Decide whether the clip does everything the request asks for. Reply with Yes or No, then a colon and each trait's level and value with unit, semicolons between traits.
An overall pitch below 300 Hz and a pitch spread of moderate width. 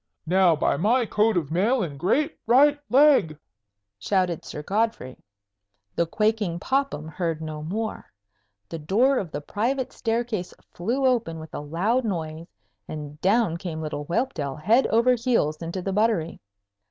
No: high, 190 Hz; wide, 6.6 semitones